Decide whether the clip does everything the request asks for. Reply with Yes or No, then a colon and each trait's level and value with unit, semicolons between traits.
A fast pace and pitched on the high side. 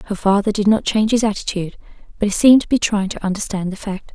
Yes: fast, 245 wpm; high, 205 Hz